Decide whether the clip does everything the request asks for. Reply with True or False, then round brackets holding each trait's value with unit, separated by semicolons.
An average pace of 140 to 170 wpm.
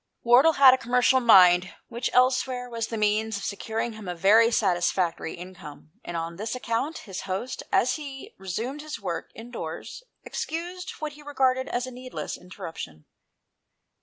True (160 wpm)